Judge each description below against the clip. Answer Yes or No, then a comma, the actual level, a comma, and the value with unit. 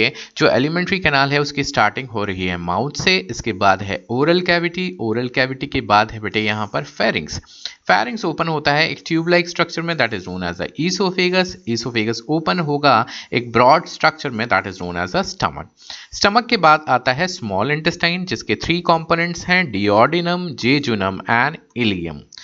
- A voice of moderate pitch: Yes, medium, 145 Hz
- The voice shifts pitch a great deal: Yes, wide, 8.0 semitones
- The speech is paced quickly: No, average, 180 wpm